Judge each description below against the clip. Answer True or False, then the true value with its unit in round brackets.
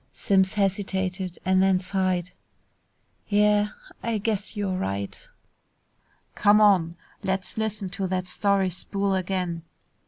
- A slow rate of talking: True (115 wpm)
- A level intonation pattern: True (1.9 semitones)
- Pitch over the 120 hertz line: True (190 Hz)